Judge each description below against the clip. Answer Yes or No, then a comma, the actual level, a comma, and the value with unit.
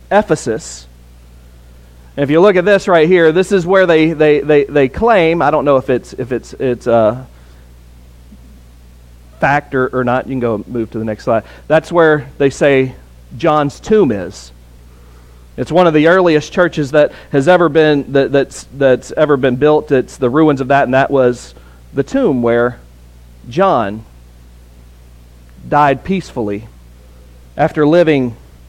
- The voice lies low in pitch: Yes, low, 130 Hz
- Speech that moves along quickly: No, average, 160 wpm